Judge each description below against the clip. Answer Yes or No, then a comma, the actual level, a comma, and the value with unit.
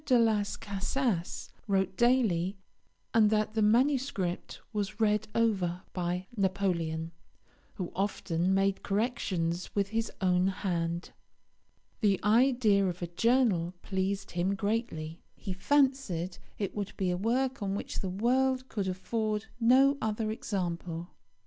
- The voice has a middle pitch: No, high, 200 Hz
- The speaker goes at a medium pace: No, slow, 130 wpm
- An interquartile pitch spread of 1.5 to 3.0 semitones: No, average, 3.9 semitones